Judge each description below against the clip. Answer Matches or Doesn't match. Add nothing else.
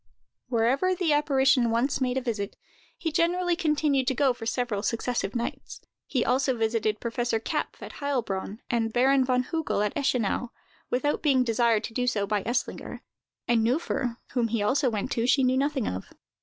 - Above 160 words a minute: Matches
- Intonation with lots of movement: Doesn't match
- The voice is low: Doesn't match